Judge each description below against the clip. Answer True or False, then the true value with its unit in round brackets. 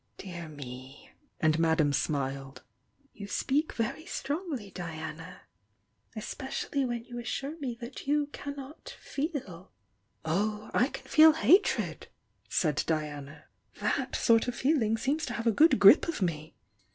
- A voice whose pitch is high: True (220 Hz)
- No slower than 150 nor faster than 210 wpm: False (140 wpm)